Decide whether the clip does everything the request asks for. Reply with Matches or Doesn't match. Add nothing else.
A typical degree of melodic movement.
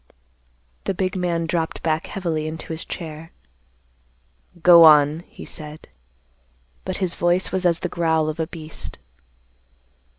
Doesn't match